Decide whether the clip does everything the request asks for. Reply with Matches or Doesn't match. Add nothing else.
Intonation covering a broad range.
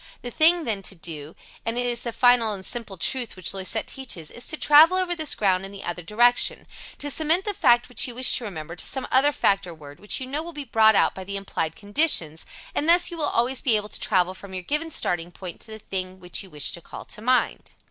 Matches